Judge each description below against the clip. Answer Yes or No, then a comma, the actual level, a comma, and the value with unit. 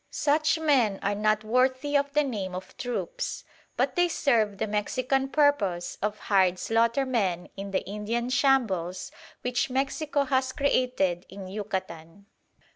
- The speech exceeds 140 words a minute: No, slow, 135 wpm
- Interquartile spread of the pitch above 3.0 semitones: Yes, wide, 5.4 semitones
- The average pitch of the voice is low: No, high, 230 Hz